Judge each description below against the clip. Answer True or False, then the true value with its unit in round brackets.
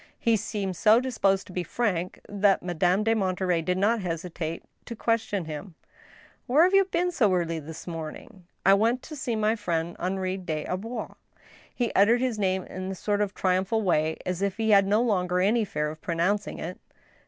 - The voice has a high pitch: True (195 Hz)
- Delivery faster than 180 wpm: True (200 wpm)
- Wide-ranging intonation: False (3.7 semitones)